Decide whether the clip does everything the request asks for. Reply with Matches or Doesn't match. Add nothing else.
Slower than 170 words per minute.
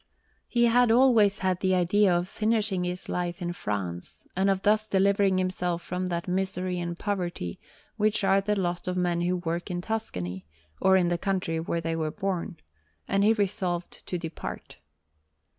Doesn't match